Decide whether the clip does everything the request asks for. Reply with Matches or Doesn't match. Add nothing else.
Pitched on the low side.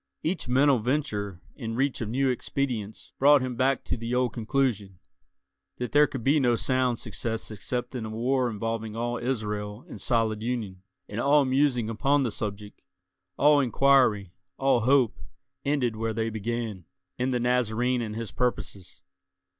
Matches